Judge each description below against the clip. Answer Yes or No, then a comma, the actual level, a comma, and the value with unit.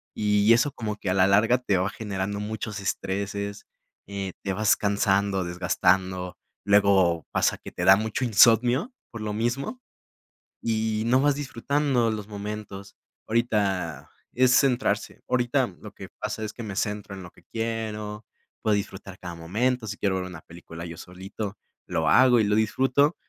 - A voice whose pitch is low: Yes, low, 105 Hz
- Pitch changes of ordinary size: Yes, average, 3.1 semitones